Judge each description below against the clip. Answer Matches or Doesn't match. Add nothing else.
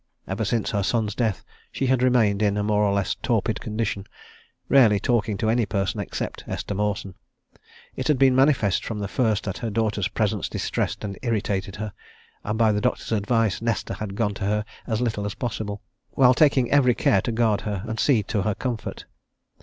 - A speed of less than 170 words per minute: Doesn't match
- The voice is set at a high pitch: Doesn't match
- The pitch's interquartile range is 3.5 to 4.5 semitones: Doesn't match